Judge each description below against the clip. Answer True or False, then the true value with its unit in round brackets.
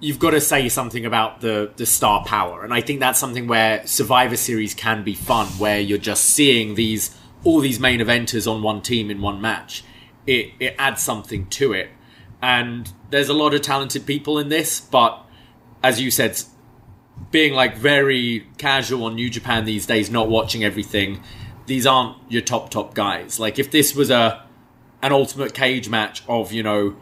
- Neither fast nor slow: True (190 wpm)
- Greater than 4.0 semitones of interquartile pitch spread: False (3.4 semitones)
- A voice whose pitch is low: True (120 Hz)